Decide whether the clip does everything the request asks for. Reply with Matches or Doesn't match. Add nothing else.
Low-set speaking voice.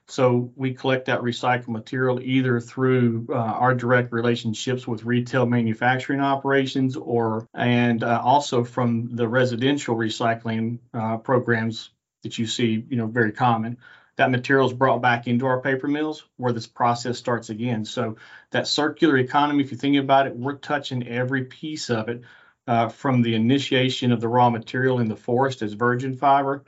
Matches